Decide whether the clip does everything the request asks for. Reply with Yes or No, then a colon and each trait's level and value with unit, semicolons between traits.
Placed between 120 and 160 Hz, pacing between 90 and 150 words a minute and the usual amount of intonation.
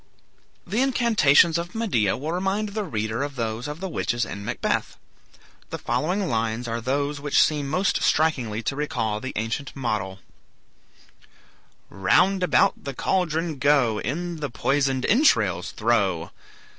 No: medium, 140 Hz; average, 140 wpm; wide, 7.3 semitones